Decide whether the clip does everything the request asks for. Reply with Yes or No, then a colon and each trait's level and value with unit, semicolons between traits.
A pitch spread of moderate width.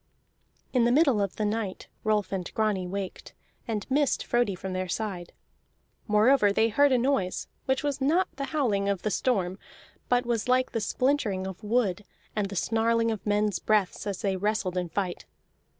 Yes: average, 3.9 semitones